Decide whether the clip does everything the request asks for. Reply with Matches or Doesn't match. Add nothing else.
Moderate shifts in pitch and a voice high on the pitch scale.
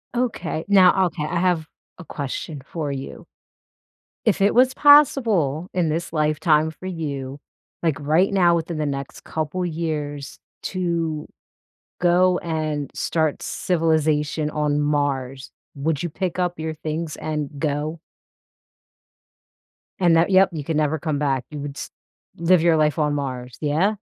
Doesn't match